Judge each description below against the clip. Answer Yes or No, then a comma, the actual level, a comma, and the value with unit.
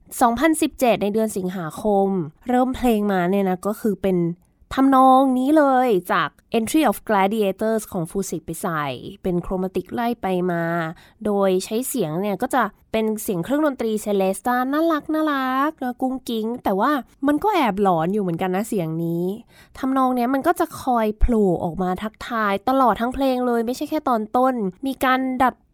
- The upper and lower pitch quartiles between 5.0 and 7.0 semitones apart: Yes, average, 5.3 semitones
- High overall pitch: Yes, high, 220 Hz